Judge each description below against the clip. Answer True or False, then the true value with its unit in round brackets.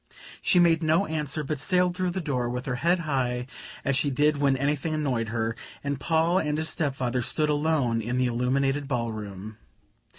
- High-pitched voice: False (140 Hz)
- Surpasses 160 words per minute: True (195 wpm)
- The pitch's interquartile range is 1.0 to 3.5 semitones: False (4.1 semitones)